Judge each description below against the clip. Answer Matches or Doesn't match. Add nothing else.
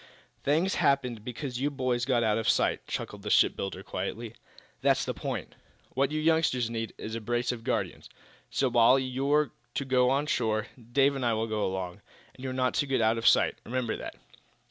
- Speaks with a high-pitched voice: Doesn't match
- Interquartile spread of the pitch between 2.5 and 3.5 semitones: Matches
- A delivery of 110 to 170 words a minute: Doesn't match